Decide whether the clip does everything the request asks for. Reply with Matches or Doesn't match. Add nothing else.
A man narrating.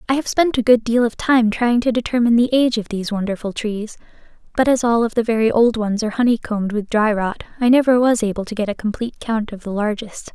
Doesn't match